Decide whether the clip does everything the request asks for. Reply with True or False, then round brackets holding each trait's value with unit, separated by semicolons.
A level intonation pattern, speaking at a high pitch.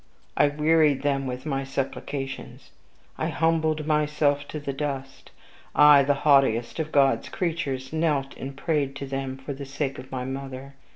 False (1.9 semitones; 140 Hz)